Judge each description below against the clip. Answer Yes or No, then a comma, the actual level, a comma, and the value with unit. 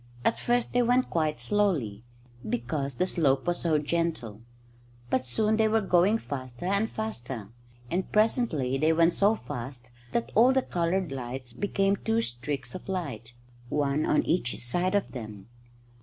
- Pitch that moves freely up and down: Yes, wide, 7.9 semitones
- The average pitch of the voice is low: No, medium, 160 Hz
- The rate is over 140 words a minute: Yes, average, 155 wpm